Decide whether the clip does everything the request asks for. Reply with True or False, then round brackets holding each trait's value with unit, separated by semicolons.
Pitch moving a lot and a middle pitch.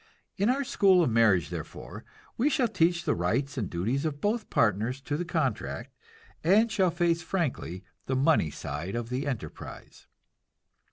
True (8.1 semitones; 145 Hz)